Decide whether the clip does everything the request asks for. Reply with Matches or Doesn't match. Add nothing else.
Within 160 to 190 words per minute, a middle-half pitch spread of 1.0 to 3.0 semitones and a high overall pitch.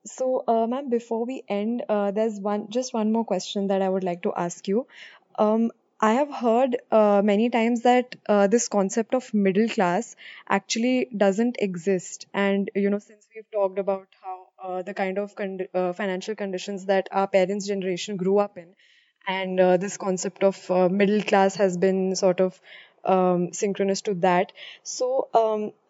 Matches